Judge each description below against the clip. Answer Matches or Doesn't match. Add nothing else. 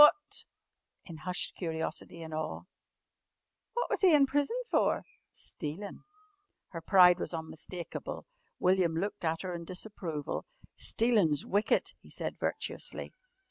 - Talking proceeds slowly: Matches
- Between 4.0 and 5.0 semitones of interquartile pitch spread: Matches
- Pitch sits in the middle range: Matches